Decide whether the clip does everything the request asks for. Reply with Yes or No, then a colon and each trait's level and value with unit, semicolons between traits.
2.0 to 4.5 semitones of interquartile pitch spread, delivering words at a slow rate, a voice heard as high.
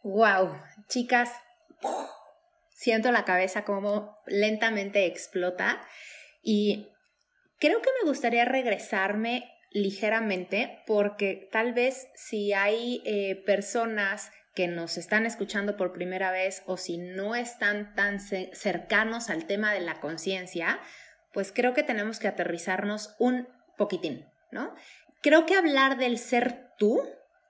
Yes: average, 3.8 semitones; slow, 120 wpm; high, 210 Hz